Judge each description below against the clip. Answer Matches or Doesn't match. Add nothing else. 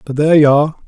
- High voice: Doesn't match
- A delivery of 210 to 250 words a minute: Doesn't match